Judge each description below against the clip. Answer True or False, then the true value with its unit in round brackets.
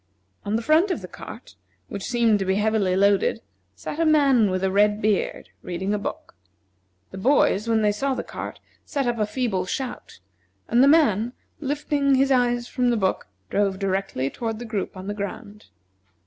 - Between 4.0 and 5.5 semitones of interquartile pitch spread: True (4.5 semitones)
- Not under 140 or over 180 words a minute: False (190 wpm)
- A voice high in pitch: True (215 Hz)